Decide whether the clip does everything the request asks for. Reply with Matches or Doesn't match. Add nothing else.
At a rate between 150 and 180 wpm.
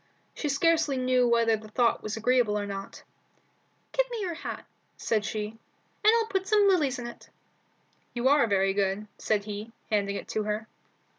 Matches